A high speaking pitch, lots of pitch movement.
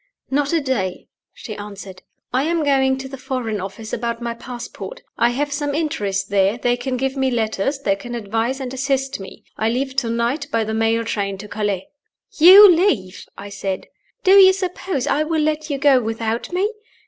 No: high, 245 Hz; average, 4.7 semitones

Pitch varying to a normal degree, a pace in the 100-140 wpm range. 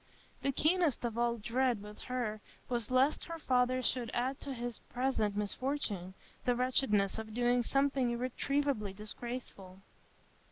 Yes: average, 3.4 semitones; slow, 135 wpm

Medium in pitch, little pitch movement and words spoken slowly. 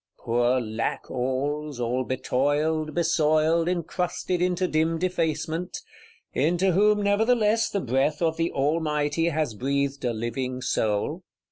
No: medium, 155 Hz; average, 4.8 semitones; slow, 115 wpm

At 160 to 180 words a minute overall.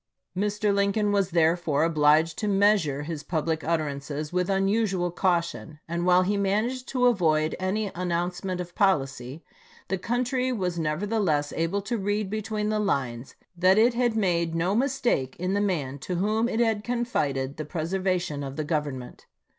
Yes: average, 165 wpm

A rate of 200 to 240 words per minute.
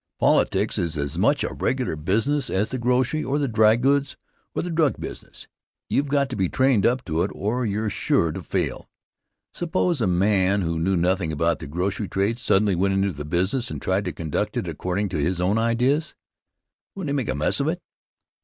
Yes: fast, 205 wpm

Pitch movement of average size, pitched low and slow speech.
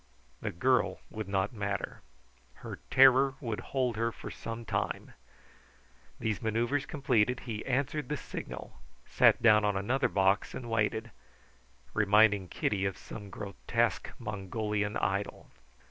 Yes: average, 3.4 semitones; low, 110 Hz; slow, 130 wpm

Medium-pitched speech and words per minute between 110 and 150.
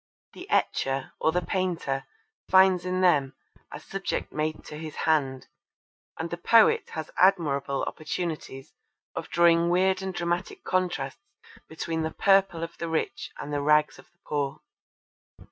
Yes: medium, 165 Hz; average, 145 wpm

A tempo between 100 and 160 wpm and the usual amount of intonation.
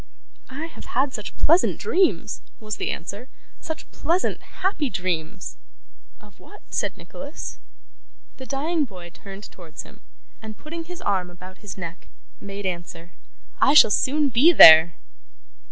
No: average, 140 wpm; wide, 8.6 semitones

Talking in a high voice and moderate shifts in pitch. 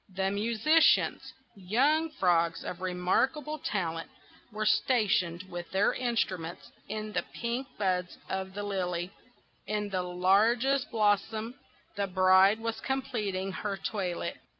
Yes: high, 200 Hz; average, 3.9 semitones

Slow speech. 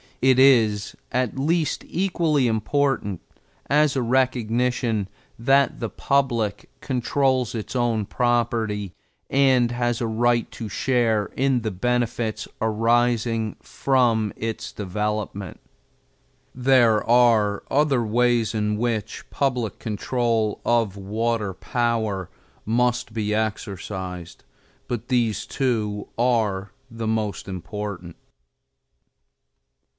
Yes: slow, 100 wpm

